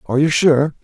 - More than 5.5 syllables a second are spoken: Yes, 6.2 syllables/s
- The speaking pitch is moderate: Yes, medium, 145 Hz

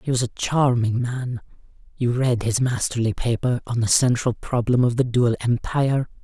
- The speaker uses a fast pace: No, average, 175 wpm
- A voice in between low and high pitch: No, low, 120 Hz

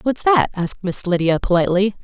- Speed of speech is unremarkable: Yes, average, 175 wpm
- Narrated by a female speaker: Yes, female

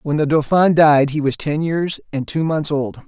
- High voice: No, medium, 150 Hz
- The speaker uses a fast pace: Yes, fast, 235 wpm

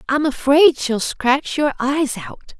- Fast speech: No, average, 160 wpm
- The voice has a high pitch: Yes, very high, 280 Hz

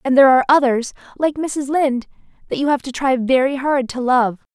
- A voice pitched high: Yes, very high, 265 Hz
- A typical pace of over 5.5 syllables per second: Yes, 5.8 syllables/s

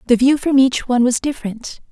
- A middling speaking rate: No, fast, 220 wpm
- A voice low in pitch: No, very high, 255 Hz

